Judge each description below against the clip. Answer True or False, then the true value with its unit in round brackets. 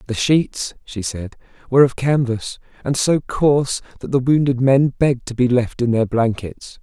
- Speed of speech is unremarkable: True (185 wpm)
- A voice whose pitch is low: True (125 Hz)